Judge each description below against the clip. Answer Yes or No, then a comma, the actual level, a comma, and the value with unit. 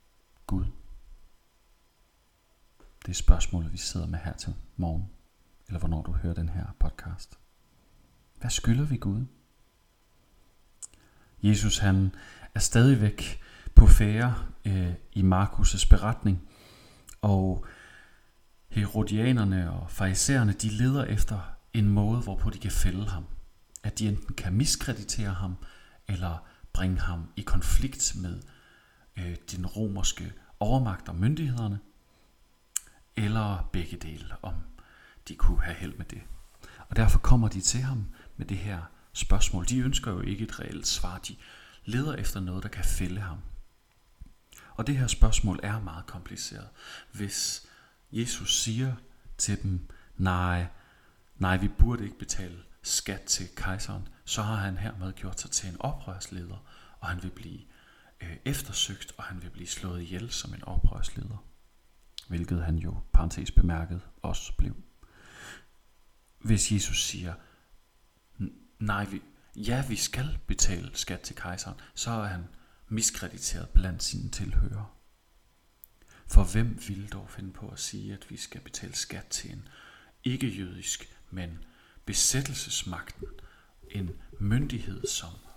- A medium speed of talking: No, slow, 130 wpm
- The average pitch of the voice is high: No, low, 100 Hz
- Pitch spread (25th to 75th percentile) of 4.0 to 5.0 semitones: No, average, 3.6 semitones